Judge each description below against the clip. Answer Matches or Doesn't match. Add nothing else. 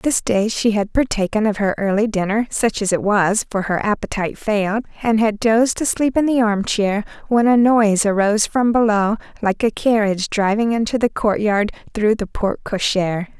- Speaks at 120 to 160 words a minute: Doesn't match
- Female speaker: Matches